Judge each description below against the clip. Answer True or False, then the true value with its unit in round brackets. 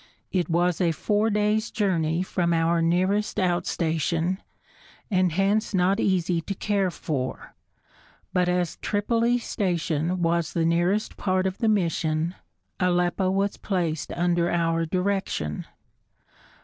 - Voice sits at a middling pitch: True (180 Hz)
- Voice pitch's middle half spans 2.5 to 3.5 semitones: True (2.8 semitones)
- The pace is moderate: False (125 wpm)